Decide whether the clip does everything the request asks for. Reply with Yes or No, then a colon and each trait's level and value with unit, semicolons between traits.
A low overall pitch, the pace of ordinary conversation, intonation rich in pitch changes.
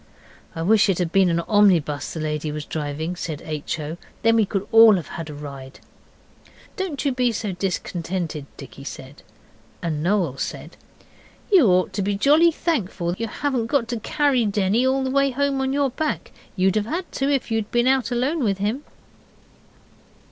No: high, 205 Hz; average, 185 wpm; wide, 7.8 semitones